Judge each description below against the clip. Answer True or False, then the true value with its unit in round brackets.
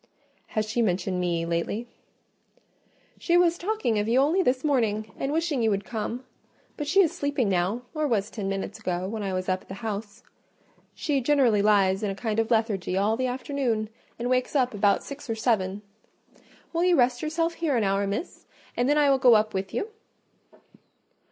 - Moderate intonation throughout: False (5.7 semitones)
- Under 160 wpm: False (195 wpm)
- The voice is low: False (225 Hz)